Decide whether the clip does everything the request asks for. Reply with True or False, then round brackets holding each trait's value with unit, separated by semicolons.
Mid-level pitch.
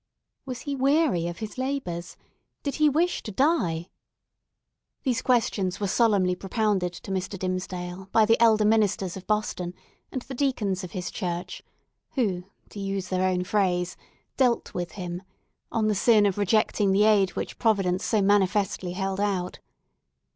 False (200 Hz)